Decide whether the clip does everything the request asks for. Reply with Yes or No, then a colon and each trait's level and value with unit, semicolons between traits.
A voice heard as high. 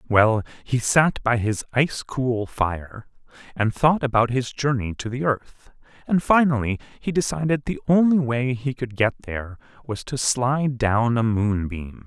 No: low, 125 Hz